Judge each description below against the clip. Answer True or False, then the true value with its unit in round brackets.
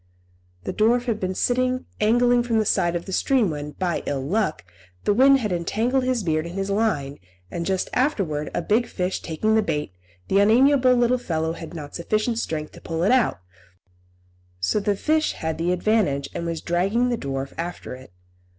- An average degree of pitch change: False (6.6 semitones)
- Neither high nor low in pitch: False (195 Hz)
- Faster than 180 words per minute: True (190 wpm)